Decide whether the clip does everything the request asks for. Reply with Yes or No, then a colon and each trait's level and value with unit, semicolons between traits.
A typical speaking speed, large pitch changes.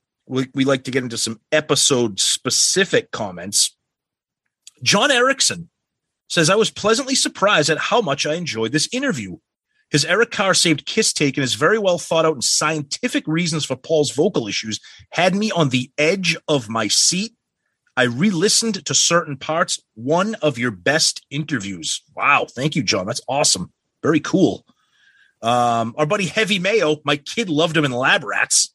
Yes: average, 170 wpm; wide, 6.3 semitones